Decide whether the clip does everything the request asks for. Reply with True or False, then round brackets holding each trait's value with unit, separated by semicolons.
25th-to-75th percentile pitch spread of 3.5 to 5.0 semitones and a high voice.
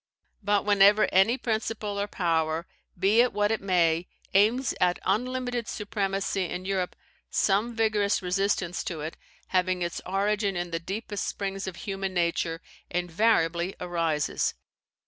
False (2.9 semitones; 195 Hz)